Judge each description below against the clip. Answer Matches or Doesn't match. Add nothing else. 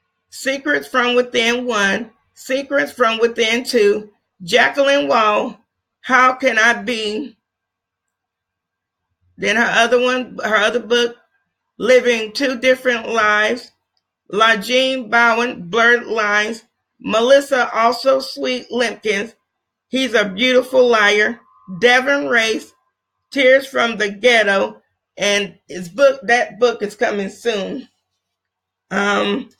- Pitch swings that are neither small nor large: Matches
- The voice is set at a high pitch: Matches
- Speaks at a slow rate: Matches